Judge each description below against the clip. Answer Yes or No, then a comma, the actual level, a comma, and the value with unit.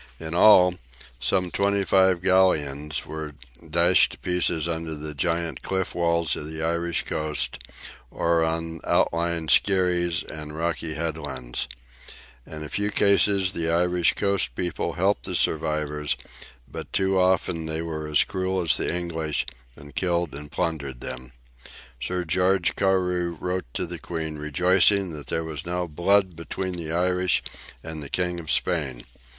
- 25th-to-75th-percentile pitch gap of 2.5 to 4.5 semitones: Yes, average, 2.8 semitones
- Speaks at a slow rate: No, average, 150 wpm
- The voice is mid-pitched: No, very low, 85 Hz